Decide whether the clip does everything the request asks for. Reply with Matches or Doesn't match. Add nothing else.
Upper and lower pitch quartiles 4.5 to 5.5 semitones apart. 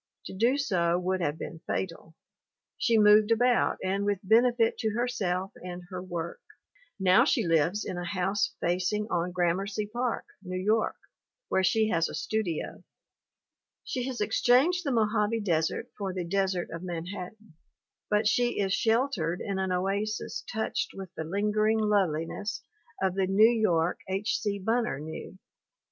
Doesn't match